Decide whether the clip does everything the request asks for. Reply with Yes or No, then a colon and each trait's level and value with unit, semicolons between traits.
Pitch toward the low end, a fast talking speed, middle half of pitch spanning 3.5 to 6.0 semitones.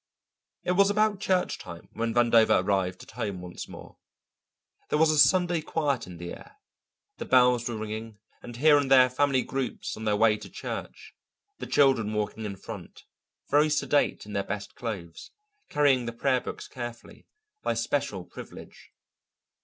No: low, 120 Hz; average, 165 wpm; average, 5.3 semitones